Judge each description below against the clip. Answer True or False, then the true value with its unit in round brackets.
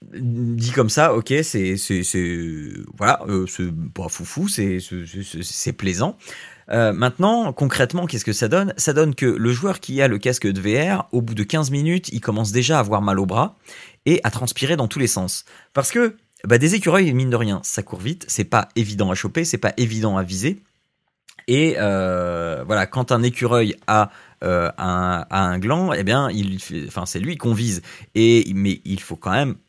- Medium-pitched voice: False (115 Hz)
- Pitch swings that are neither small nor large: False (6.1 semitones)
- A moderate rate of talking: True (210 wpm)